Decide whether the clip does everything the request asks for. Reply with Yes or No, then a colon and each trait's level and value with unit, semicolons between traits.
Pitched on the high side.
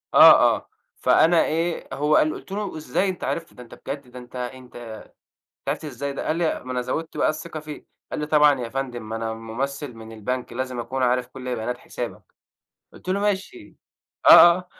No: low, 135 Hz